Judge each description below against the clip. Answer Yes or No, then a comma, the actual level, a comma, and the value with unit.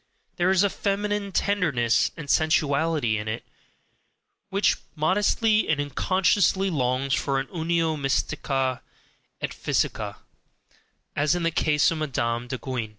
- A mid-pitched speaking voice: Yes, medium, 155 Hz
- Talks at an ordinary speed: No, slow, 130 wpm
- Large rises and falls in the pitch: Yes, wide, 5.7 semitones